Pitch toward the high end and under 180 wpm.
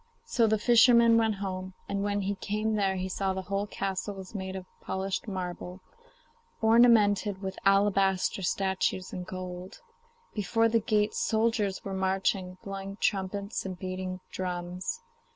Yes: high, 195 Hz; average, 145 wpm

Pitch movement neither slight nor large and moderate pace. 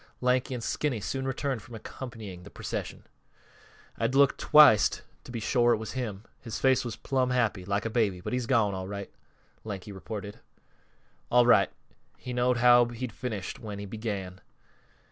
Yes: average, 3.7 semitones; average, 180 wpm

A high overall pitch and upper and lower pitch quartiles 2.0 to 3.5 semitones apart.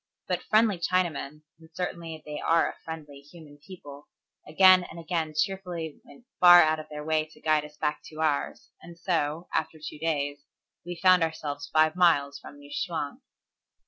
No: medium, 160 Hz; narrow, 2.6 semitones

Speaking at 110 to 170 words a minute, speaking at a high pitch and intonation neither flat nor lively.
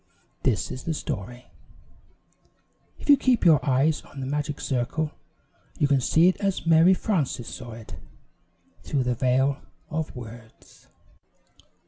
No: slow, 135 wpm; medium, 140 Hz; average, 4.3 semitones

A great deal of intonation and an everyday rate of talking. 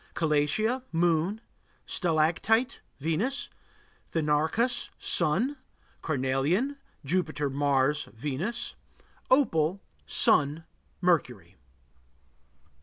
No: wide, 6.6 semitones; slow, 60 wpm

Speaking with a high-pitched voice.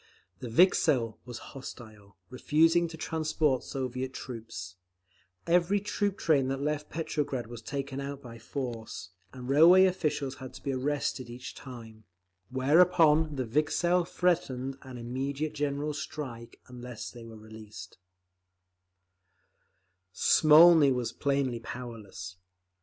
No: low, 135 Hz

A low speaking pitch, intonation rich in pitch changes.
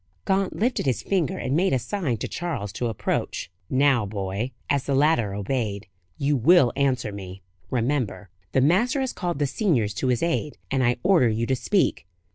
Yes: low, 130 Hz; wide, 7.1 semitones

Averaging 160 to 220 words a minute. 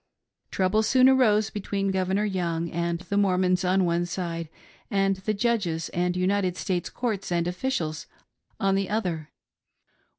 No: average, 140 wpm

